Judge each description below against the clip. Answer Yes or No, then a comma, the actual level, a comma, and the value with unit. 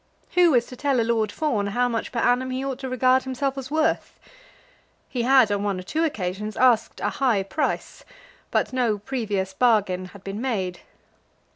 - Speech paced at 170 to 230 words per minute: Yes, average, 185 wpm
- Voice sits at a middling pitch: No, high, 240 Hz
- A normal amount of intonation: Yes, average, 4.3 semitones